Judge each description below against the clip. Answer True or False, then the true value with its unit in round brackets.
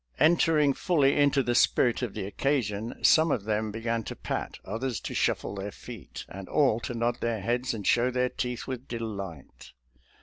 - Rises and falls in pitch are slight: False (3.6 semitones)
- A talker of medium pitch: False (120 Hz)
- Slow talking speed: False (190 wpm)